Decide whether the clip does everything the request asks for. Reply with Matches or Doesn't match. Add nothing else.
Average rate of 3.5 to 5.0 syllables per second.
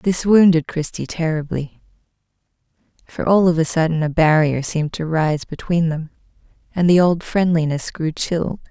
Matches